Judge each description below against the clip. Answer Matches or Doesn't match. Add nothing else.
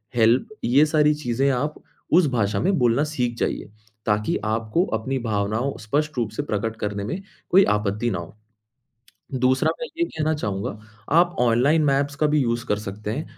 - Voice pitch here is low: Matches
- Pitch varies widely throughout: Matches